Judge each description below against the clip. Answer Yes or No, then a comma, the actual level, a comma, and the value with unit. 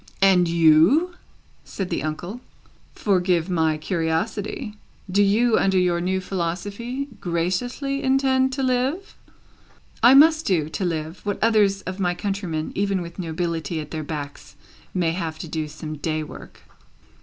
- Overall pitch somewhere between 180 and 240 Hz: Yes, medium, 185 Hz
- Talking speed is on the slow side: No, average, 145 wpm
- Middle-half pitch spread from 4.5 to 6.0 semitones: Yes, average, 4.9 semitones